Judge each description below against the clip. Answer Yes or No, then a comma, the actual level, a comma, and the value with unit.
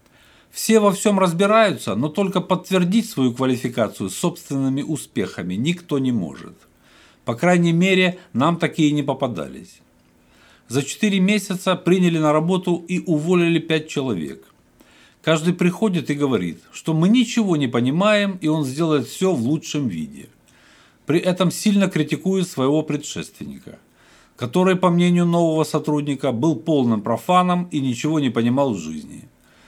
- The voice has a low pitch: No, medium, 160 Hz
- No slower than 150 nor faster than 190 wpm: No, average, 135 wpm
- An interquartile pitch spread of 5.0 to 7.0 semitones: No, average, 4.5 semitones